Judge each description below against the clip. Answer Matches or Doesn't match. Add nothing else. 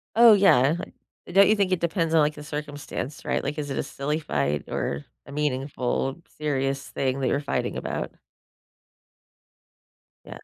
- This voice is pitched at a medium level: Matches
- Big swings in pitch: Doesn't match